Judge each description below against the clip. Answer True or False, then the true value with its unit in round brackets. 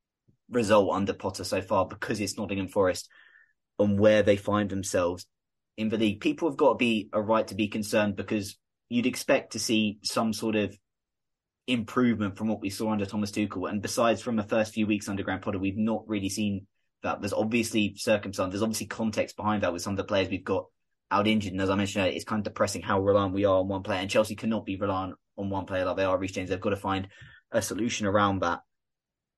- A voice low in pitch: True (100 Hz)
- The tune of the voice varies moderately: False (2.0 semitones)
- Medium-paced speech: False (225 wpm)